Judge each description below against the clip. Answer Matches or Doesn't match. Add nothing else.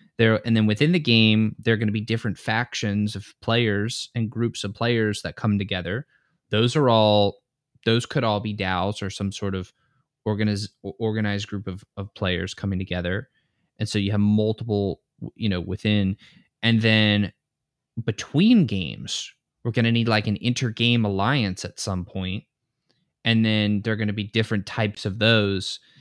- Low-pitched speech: Matches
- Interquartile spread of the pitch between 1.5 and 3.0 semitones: Matches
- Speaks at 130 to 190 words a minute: Matches